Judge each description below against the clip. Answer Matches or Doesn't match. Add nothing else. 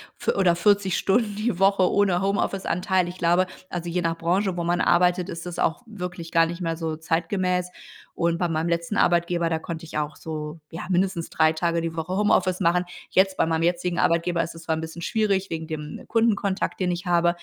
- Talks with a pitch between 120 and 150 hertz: Doesn't match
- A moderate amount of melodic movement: Doesn't match